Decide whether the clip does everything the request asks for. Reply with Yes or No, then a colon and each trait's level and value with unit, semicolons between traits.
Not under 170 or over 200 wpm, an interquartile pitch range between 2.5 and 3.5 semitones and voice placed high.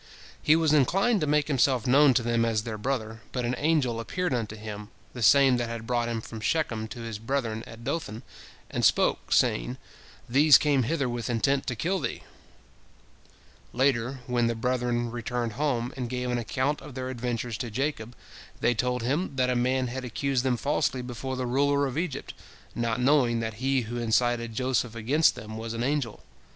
No: average, 190 wpm; average, 2.9 semitones; low, 125 Hz